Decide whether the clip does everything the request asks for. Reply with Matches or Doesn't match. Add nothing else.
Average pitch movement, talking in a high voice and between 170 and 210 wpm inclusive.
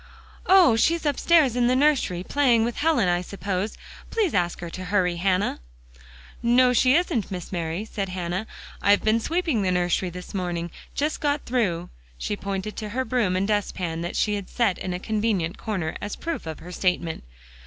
Doesn't match